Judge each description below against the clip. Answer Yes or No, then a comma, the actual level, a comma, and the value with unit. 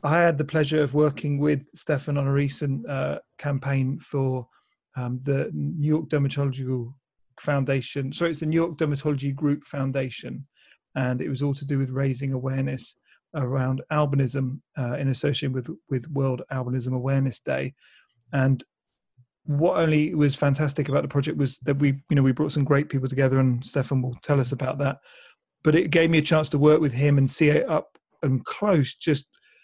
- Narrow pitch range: Yes, narrow, 2.2 semitones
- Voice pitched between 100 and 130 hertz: No, medium, 140 Hz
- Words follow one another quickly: No, average, 185 wpm